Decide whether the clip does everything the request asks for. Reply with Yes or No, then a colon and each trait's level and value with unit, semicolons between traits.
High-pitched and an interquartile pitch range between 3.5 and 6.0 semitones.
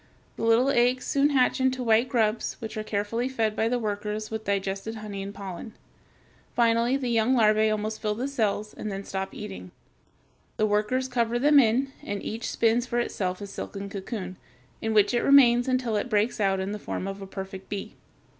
No: high, 220 Hz; average, 3.0 semitones